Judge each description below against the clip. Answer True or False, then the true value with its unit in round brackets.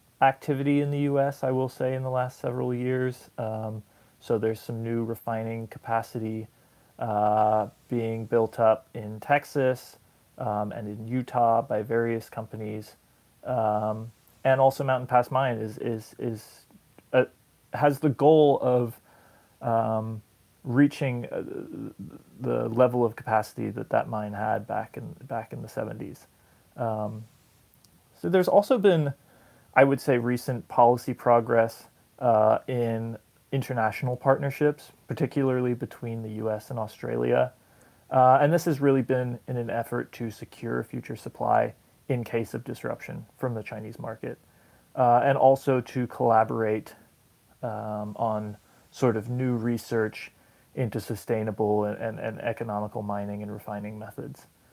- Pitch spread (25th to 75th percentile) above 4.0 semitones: False (3.1 semitones)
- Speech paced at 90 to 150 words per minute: True (140 wpm)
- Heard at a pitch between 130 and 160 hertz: False (120 Hz)